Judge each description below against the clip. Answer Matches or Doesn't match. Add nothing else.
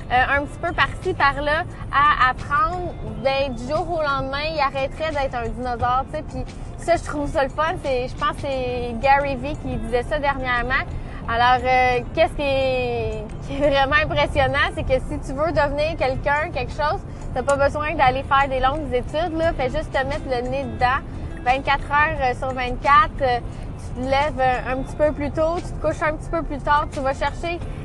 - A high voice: Matches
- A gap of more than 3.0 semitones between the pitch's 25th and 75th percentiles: Doesn't match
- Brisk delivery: Doesn't match